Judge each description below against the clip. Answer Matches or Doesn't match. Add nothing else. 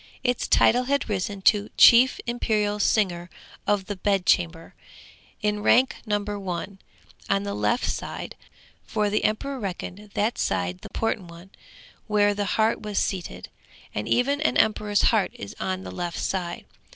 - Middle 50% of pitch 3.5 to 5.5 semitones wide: Doesn't match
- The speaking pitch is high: Matches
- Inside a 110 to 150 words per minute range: Doesn't match